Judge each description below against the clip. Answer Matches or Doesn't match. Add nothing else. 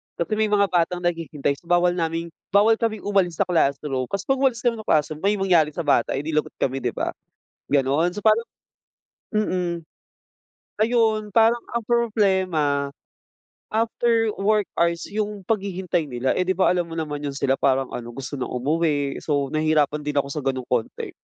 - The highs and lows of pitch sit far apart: Matches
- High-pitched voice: Doesn't match